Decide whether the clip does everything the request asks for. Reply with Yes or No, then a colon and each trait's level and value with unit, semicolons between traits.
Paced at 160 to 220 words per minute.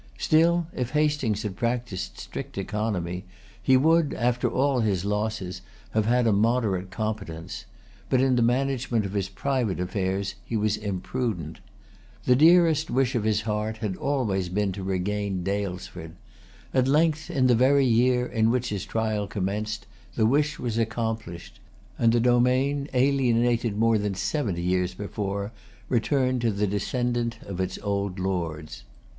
No: average, 150 wpm